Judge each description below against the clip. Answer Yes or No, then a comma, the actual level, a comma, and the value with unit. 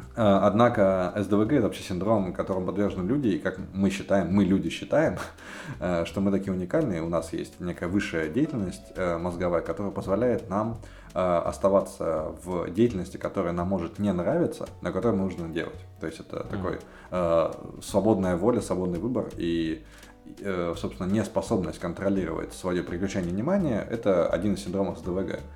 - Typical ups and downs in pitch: No, narrow, 2.2 semitones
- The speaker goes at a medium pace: Yes, average, 145 wpm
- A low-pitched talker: Yes, very low, 95 Hz